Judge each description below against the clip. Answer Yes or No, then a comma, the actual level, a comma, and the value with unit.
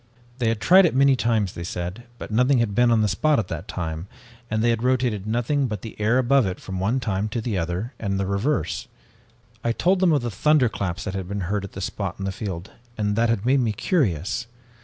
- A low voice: Yes, low, 110 Hz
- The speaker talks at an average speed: No, fast, 245 wpm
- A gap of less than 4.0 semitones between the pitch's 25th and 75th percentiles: No, average, 4.3 semitones